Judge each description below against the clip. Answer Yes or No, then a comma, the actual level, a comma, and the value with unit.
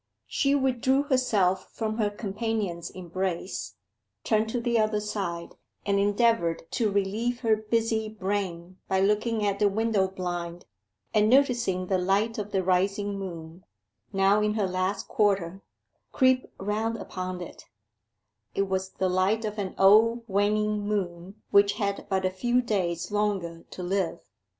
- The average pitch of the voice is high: Yes, high, 200 Hz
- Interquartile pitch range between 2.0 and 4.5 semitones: Yes, average, 2.8 semitones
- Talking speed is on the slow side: No, average, 145 wpm